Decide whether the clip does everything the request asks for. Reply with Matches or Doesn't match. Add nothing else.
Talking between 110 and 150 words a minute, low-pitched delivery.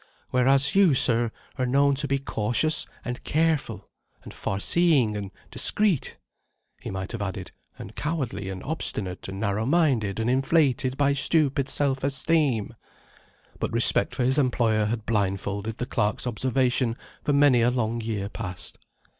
Matches